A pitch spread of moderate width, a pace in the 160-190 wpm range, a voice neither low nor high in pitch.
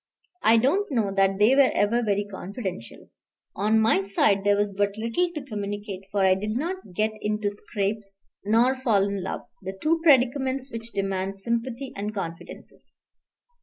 No: average, 3.5 semitones; average, 165 wpm; high, 210 Hz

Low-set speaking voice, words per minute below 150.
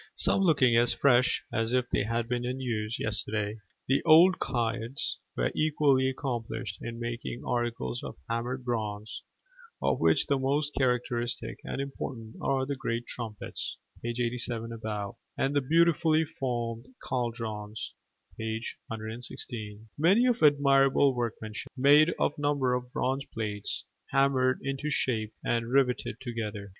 Yes: low, 120 Hz; average, 140 wpm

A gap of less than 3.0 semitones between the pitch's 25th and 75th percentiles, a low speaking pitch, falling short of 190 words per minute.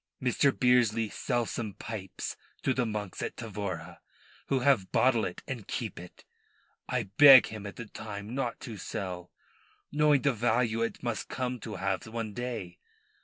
No: average, 3.6 semitones; low, 115 Hz; average, 165 wpm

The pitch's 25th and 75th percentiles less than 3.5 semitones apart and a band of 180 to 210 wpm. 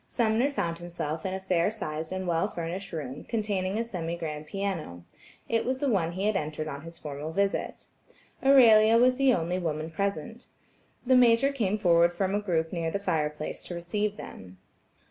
No: average, 4.9 semitones; average, 185 wpm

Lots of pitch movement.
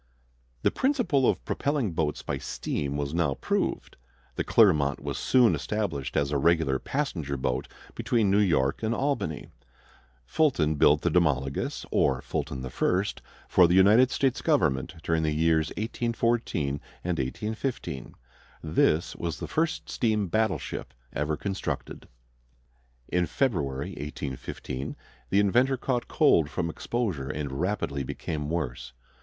Yes: wide, 7.7 semitones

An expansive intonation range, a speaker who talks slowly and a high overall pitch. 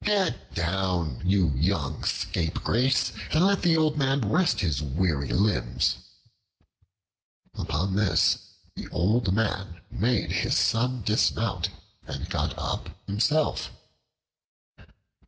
No: wide, 6.9 semitones; slow, 105 wpm; low, 100 Hz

